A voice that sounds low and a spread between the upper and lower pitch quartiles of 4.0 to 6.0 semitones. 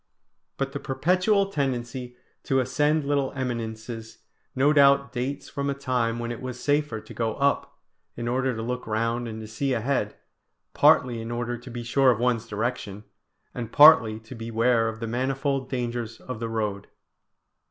No: low, 125 Hz; average, 3.2 semitones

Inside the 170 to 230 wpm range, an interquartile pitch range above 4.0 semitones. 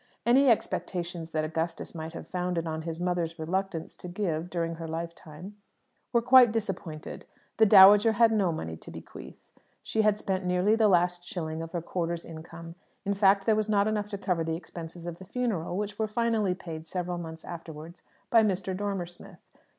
No: average, 185 wpm; average, 3.7 semitones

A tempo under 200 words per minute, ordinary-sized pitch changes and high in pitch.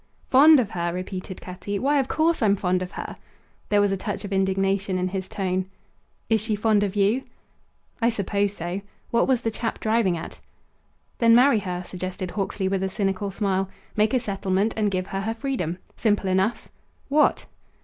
Yes: average, 185 wpm; average, 3.1 semitones; high, 200 Hz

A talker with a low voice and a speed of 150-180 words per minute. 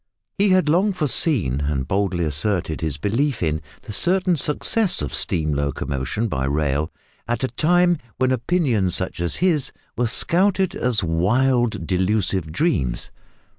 No: low, 110 Hz; average, 140 wpm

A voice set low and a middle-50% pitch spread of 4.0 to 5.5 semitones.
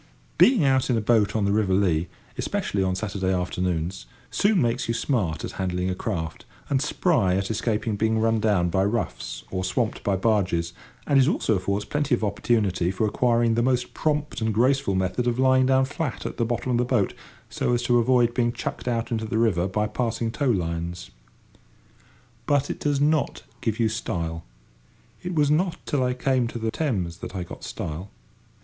Yes: low, 110 Hz; average, 5.0 semitones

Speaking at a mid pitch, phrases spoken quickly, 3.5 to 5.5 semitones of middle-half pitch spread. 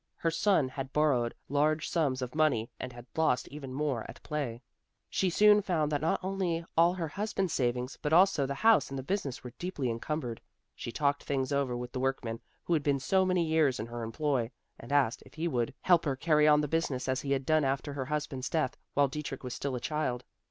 Yes: medium, 145 Hz; fast, 220 wpm; average, 3.8 semitones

